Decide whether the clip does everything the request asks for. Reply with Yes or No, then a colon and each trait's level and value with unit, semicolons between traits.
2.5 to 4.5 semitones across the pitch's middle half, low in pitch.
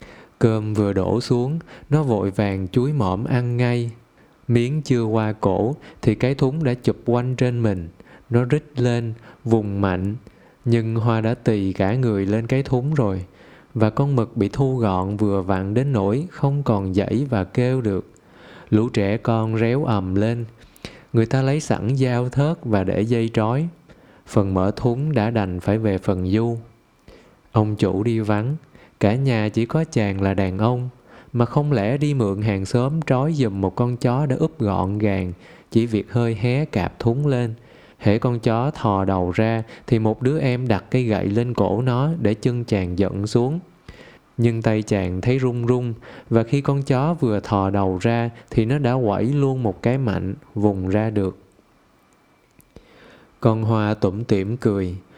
Yes: average, 3.7 semitones; low, 115 Hz